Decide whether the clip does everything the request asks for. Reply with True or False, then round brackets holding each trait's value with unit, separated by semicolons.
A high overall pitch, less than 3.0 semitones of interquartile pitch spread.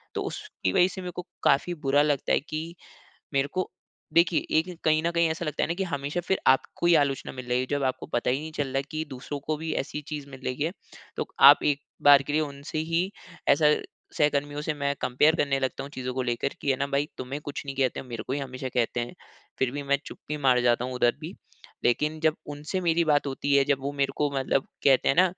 False (145 Hz; 2.6 semitones)